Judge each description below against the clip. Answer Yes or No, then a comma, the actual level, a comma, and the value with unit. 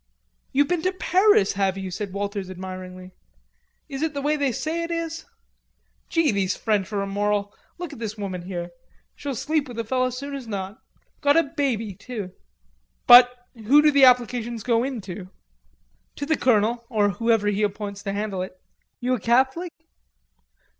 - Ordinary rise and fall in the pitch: No, wide, 5.8 semitones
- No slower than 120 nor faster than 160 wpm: No, average, 175 wpm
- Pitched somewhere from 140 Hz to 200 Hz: No, high, 230 Hz